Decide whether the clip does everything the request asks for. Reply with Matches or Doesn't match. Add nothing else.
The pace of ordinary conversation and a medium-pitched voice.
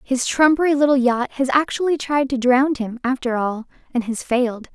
Doesn't match